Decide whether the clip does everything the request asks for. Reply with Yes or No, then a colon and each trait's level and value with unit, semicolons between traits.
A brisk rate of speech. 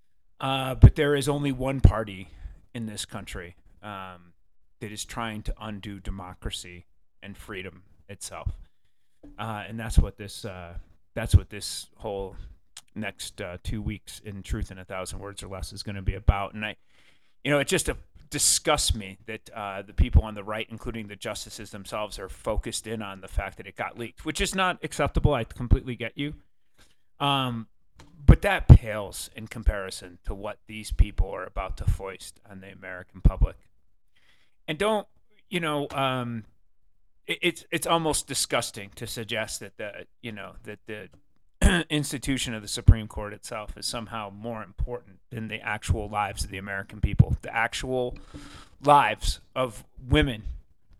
No: average, 170 wpm